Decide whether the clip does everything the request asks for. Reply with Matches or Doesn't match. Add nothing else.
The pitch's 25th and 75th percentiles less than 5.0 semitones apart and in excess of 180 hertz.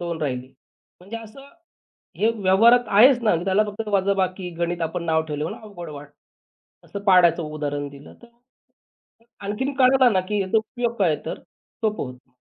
Doesn't match